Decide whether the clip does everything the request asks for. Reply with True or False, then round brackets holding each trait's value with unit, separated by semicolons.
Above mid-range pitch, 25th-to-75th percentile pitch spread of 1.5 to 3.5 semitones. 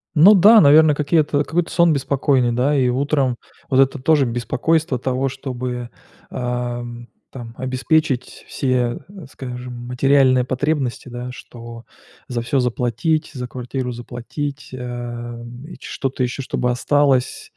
False (130 Hz; 2.7 semitones)